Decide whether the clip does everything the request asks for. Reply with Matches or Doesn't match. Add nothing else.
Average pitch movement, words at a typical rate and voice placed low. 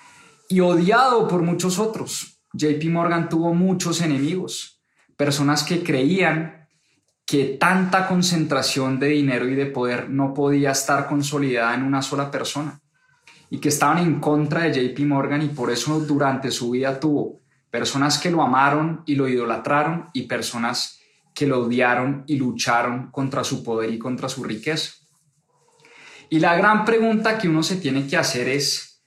Doesn't match